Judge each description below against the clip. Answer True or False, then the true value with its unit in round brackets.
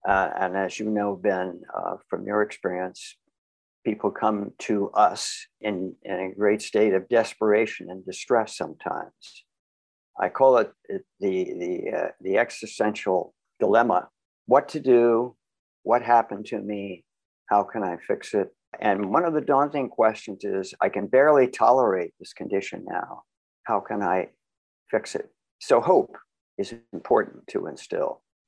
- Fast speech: False (150 wpm)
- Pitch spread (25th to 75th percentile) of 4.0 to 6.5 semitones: True (4.3 semitones)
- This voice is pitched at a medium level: False (105 Hz)